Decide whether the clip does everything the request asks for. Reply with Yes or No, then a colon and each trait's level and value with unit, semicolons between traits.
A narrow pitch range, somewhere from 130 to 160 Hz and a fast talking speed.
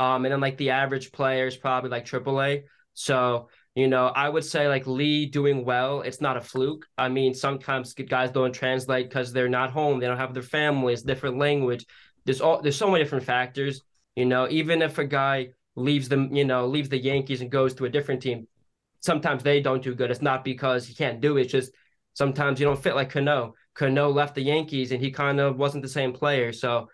Yes: narrow, 1.8 semitones; low, 135 Hz; fast, 225 wpm